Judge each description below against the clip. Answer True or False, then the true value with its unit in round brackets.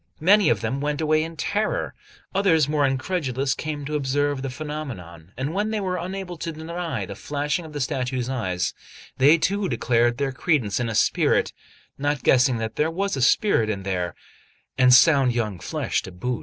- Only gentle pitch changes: False (4.7 semitones)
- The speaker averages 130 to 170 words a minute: False (185 wpm)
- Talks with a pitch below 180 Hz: True (140 Hz)